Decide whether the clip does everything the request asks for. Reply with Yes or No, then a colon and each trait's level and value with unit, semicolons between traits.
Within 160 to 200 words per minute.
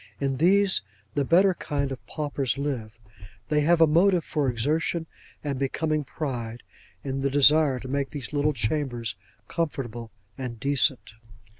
No: average, 145 wpm